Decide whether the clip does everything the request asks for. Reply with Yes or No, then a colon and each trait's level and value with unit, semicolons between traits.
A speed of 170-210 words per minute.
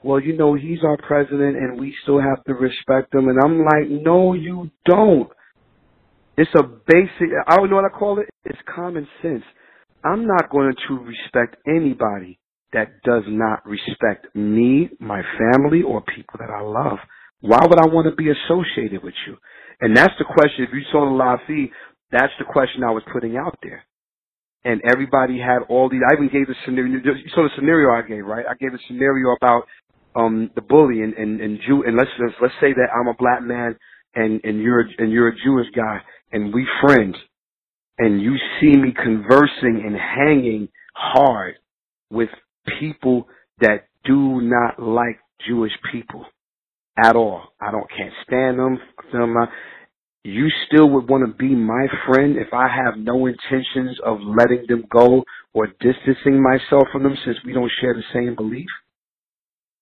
Yes: average, 180 wpm